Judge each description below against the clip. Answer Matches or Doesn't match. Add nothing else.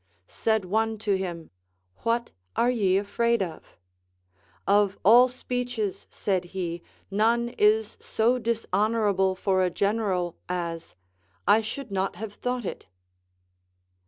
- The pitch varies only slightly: Doesn't match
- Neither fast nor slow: Doesn't match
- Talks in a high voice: Matches